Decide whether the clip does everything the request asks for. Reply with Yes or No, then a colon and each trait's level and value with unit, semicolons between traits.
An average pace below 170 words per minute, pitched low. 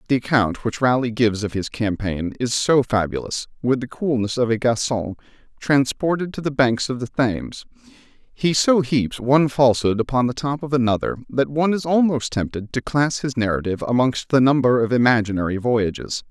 No: average, 180 wpm; low, 125 Hz